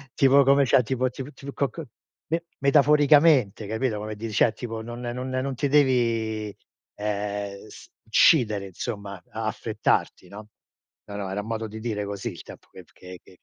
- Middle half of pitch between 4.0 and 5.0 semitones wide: Yes, average, 4.4 semitones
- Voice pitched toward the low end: Yes, low, 115 Hz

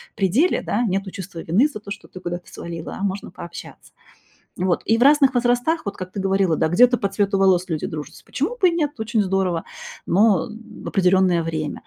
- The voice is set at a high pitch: Yes, high, 195 Hz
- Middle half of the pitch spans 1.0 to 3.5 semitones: No, average, 4.3 semitones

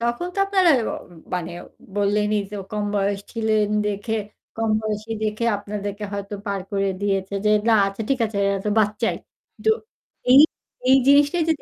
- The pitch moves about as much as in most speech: No, narrow, 2.2 semitones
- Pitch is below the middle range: No, high, 210 Hz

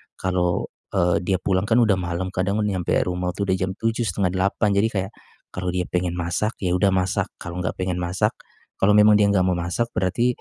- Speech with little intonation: Yes, narrow, 2.1 semitones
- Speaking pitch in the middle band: No, very low, 95 Hz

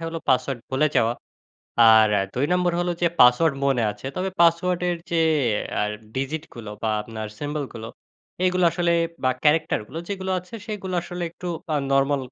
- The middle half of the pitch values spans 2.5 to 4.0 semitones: No, wide, 5.4 semitones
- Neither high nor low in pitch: Yes, medium, 155 Hz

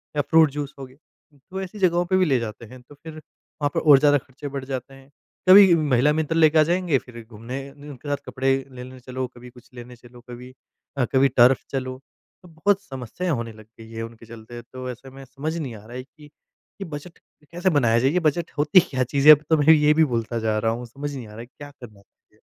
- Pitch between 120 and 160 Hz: Yes, low, 135 Hz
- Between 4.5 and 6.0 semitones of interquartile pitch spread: No, average, 3.9 semitones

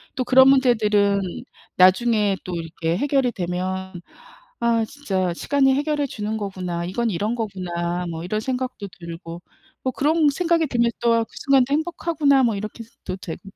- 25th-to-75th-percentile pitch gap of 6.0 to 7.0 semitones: Yes, wide, 6.3 semitones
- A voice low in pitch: No, high, 220 Hz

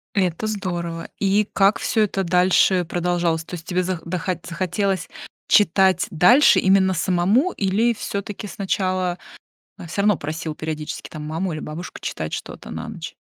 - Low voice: No, medium, 185 Hz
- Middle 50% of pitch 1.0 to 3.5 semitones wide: Yes, average, 2.7 semitones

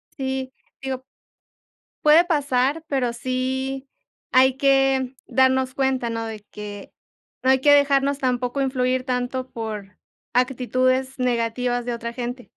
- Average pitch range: No, narrow, 1.4 semitones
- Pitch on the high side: Yes, very high, 260 Hz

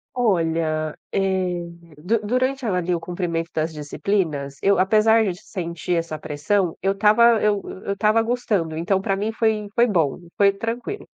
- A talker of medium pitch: No, high, 195 Hz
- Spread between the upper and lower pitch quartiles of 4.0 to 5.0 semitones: Yes, average, 4.6 semitones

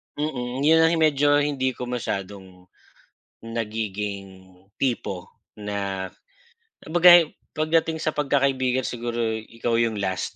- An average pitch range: No, wide, 6.2 semitones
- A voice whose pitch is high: No, low, 120 Hz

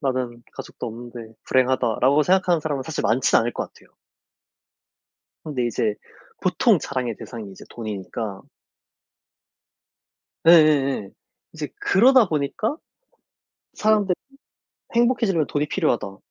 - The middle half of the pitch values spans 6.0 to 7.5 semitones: Yes, wide, 6.3 semitones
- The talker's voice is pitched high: No, low, 135 Hz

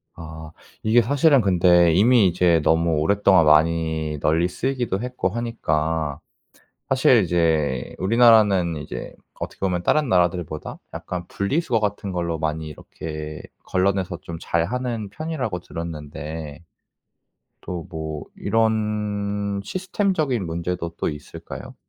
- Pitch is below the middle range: Yes, very low, 90 Hz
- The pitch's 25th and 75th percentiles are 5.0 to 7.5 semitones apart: Yes, average, 5.3 semitones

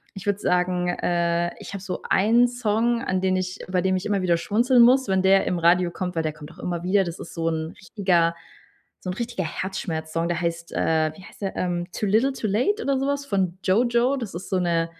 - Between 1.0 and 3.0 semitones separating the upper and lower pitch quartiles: No, average, 3.7 semitones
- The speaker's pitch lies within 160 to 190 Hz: Yes, medium, 185 Hz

